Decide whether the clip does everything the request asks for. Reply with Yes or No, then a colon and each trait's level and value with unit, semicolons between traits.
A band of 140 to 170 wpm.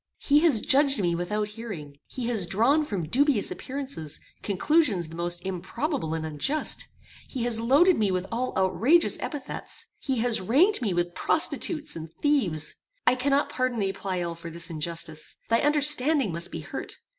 Yes: average, 165 wpm